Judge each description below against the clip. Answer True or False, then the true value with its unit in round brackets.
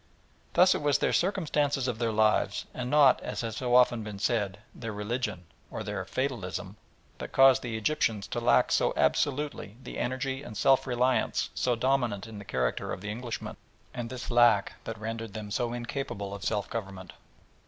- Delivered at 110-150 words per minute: False (180 wpm)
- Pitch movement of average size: True (3.7 semitones)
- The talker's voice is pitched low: True (120 Hz)